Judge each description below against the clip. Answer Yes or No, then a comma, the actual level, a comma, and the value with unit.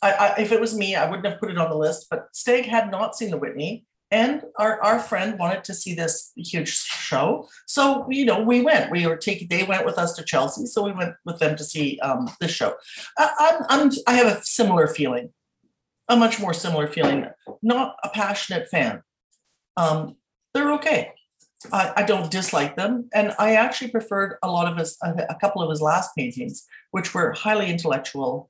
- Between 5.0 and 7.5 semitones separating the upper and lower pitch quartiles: Yes, wide, 5.4 semitones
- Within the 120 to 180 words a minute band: No, fast, 205 wpm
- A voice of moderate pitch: No, high, 205 Hz